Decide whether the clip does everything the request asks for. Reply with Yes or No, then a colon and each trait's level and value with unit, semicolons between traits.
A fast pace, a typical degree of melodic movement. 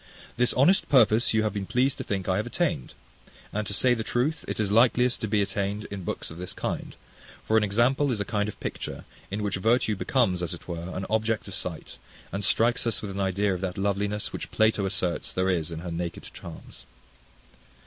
Yes: fast, 220 wpm; average, 3.1 semitones